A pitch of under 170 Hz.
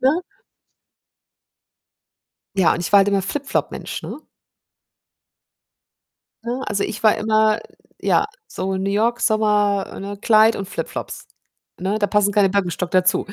No: high, 205 Hz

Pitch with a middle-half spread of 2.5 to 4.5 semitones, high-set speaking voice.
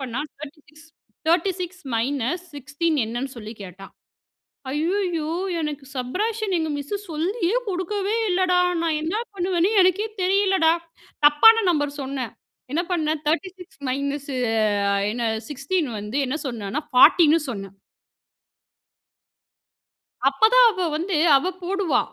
No: average, 5.1 semitones; very high, 315 Hz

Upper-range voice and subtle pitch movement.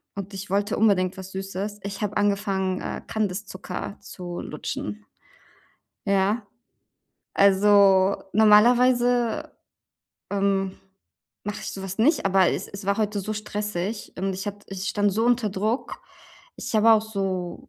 Yes: high, 200 Hz; narrow, 1.9 semitones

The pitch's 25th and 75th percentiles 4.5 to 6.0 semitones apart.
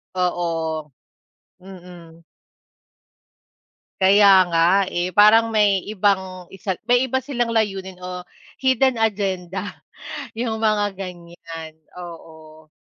No: average, 3.6 semitones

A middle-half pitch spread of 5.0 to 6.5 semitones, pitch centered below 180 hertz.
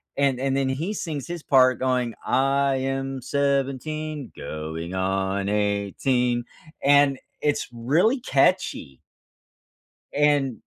No: average, 3.2 semitones; low, 135 Hz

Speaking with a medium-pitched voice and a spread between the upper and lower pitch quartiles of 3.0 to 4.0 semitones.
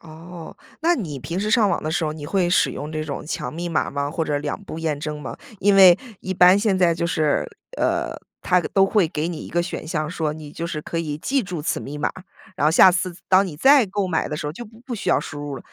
Yes: medium, 170 Hz; average, 3.7 semitones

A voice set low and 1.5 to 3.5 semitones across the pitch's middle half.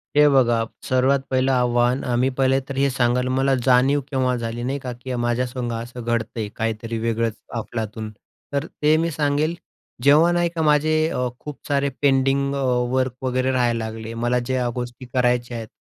Yes: low, 125 Hz; narrow, 2.4 semitones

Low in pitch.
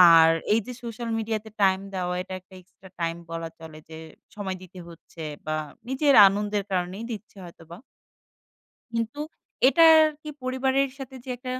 No: high, 205 Hz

